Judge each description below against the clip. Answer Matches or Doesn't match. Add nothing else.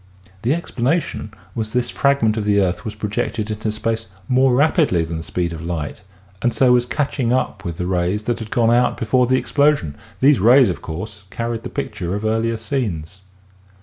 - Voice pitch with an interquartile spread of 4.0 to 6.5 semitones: Matches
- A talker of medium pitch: Doesn't match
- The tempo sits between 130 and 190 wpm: Doesn't match